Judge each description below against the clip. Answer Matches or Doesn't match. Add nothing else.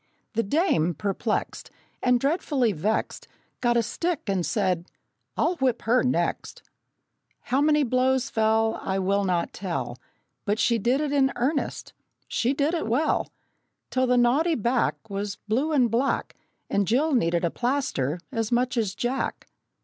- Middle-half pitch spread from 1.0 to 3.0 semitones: Doesn't match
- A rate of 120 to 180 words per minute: Matches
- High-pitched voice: Matches